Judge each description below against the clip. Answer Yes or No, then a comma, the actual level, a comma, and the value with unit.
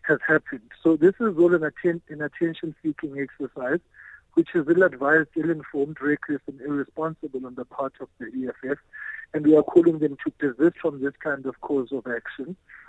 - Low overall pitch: No, medium, 155 Hz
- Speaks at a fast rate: No, average, 190 wpm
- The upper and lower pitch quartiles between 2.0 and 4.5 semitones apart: Yes, average, 3.4 semitones